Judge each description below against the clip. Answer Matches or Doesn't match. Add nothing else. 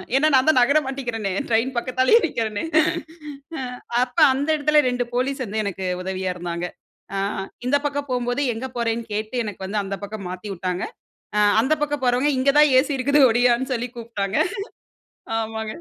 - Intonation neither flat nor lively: Matches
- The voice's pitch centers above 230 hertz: Matches